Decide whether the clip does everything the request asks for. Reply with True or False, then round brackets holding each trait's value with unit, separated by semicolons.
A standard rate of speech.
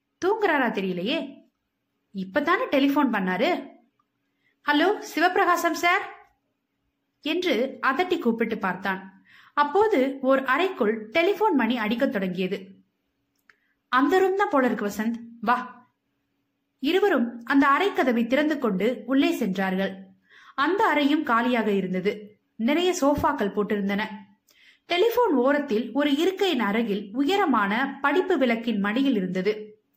True (85 wpm)